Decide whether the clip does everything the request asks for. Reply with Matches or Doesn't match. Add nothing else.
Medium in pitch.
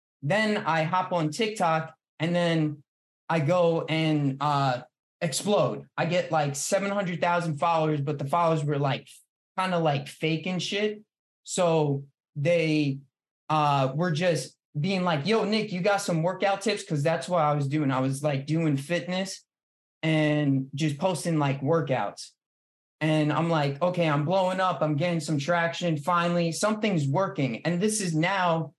Matches